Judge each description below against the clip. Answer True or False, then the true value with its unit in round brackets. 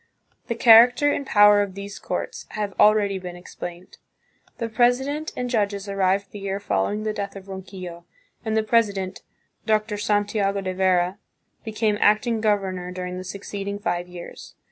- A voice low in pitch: False (200 Hz)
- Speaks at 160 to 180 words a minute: True (170 wpm)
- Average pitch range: False (2.3 semitones)